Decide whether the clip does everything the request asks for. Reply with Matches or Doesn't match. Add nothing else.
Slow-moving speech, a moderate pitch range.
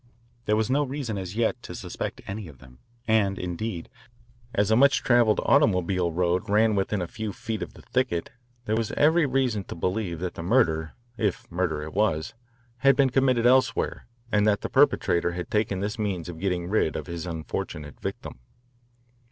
Doesn't match